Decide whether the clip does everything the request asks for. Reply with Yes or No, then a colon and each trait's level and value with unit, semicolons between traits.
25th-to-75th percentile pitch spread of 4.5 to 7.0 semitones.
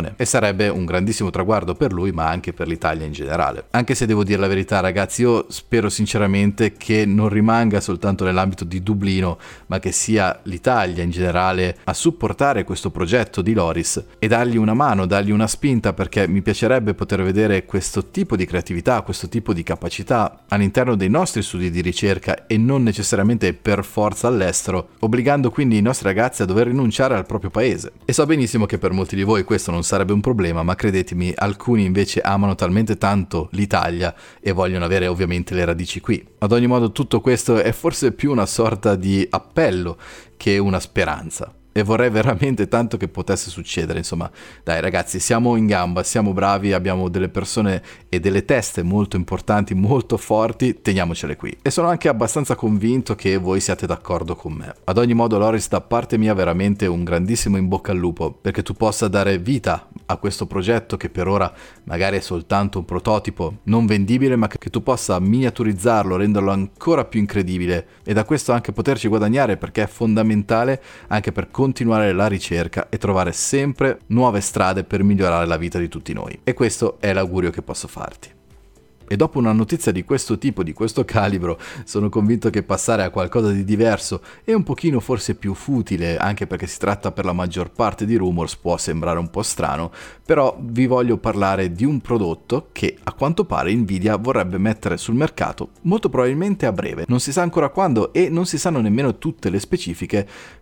No: average, 3.8 semitones